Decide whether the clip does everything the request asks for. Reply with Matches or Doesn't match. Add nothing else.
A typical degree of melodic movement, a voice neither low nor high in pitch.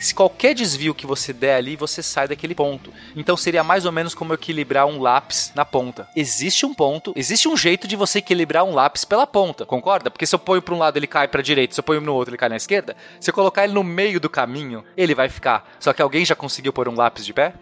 Matches